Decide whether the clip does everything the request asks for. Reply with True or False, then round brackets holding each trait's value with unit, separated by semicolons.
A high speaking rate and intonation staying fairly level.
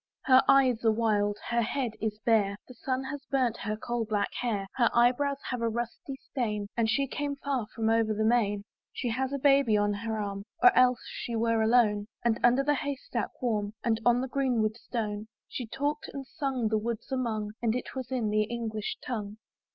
False (210 wpm; 3.2 semitones)